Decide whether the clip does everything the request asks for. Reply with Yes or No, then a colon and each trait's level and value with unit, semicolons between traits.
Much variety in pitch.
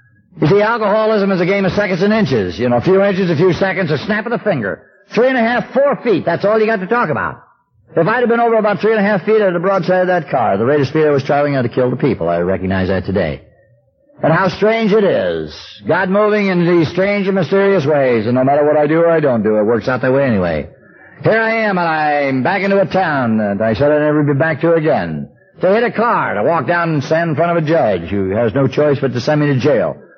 Yes: wide, 6.9 semitones